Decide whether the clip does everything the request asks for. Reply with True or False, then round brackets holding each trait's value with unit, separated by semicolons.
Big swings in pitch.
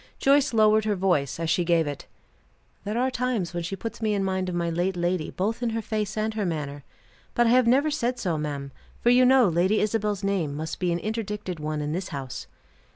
False (5.0 semitones)